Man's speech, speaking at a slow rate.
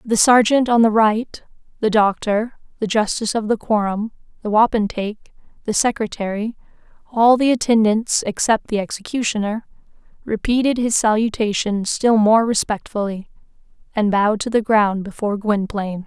No: female; slow, 130 wpm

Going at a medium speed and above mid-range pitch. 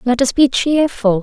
Yes: average, 195 wpm; very high, 255 Hz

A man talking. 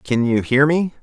Yes: male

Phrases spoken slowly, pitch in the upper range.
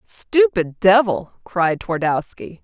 Yes: slow, 90 wpm; high, 195 Hz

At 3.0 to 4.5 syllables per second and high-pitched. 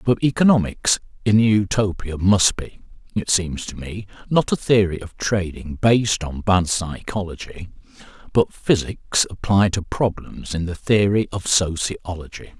No: 4.3 syllables/s; very low, 95 Hz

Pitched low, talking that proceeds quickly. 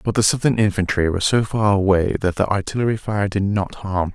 Yes: low, 100 Hz; fast, 215 wpm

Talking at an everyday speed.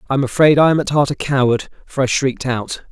No: fast, 270 wpm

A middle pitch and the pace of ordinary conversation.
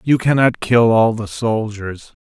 No: low, 115 Hz; average, 160 wpm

